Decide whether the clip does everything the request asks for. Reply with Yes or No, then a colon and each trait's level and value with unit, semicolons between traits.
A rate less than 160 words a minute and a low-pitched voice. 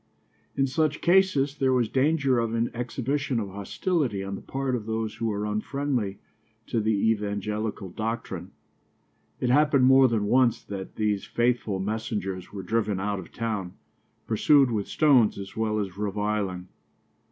Yes: average, 150 wpm; low, 110 Hz